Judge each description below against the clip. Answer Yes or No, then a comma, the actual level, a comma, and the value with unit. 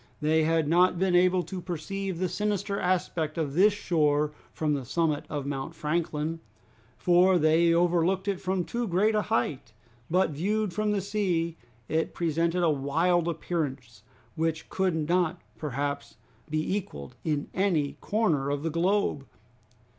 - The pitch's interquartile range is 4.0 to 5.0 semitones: No, average, 3.5 semitones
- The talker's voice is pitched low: No, medium, 170 Hz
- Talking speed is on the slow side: No, average, 150 wpm